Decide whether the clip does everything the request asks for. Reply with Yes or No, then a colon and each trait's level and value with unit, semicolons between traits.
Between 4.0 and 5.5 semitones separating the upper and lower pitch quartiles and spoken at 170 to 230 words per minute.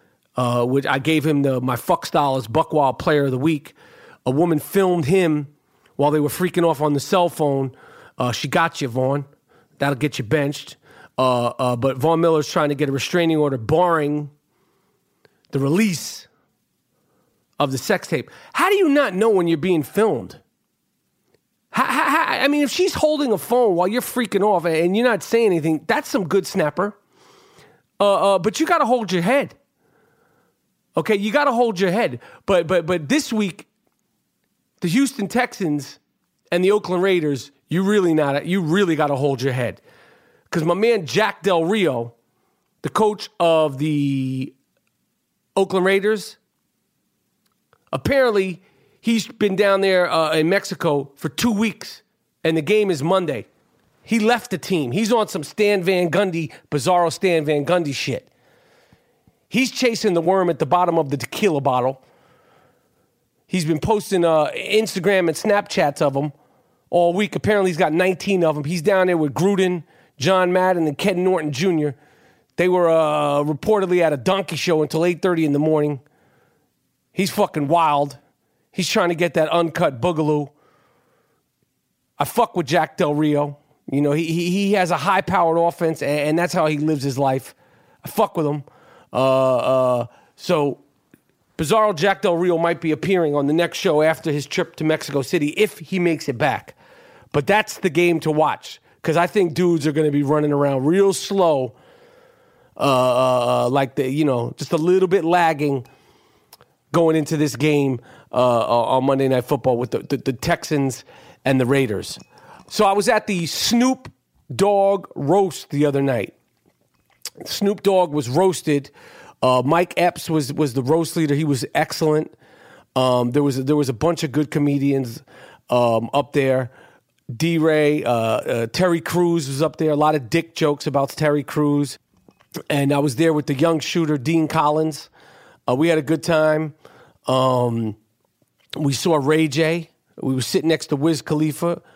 Yes: average, 4.6 semitones; average, 175 wpm